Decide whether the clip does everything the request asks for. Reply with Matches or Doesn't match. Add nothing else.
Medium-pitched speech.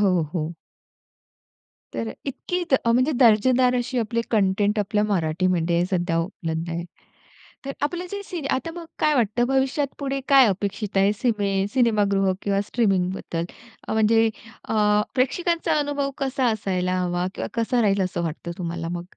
Doesn't match